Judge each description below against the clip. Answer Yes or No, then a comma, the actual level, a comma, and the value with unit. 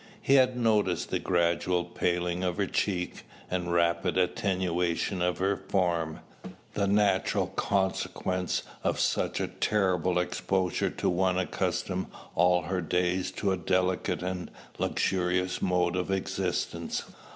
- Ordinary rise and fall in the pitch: No, narrow, 1.3 semitones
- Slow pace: Yes, slow, 130 wpm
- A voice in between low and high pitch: No, very low, 90 Hz